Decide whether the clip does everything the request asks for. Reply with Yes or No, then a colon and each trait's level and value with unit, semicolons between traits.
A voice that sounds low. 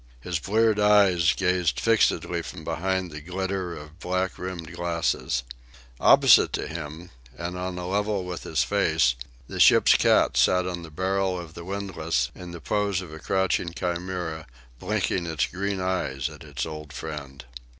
Yes: very low, 90 Hz